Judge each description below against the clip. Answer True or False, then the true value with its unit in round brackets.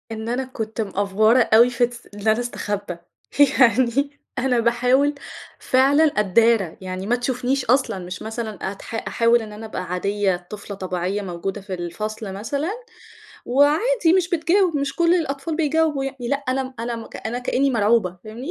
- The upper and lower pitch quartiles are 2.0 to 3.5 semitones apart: False (4.8 semitones)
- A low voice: False (235 Hz)